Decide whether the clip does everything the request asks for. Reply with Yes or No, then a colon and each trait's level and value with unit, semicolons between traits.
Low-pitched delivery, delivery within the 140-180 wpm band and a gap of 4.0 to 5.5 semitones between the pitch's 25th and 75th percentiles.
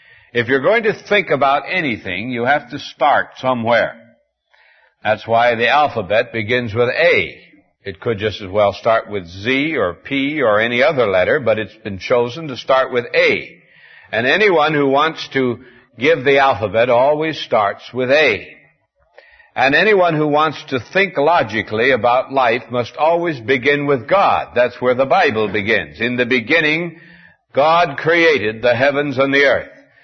Yes: low, 130 Hz; average, 165 wpm; average, 4.3 semitones